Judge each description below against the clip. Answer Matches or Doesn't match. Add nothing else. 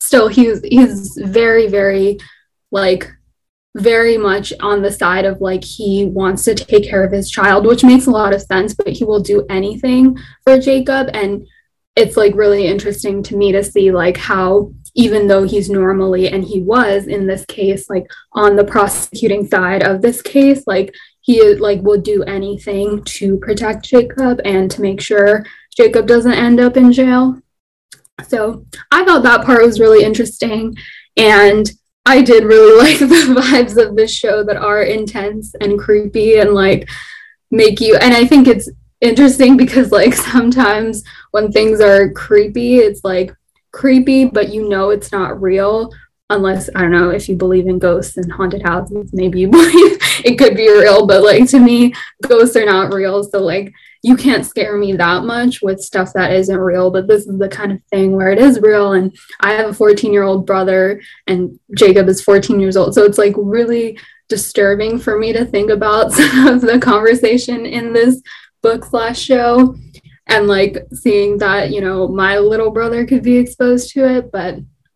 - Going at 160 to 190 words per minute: Matches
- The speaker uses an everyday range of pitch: Matches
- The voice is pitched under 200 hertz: Doesn't match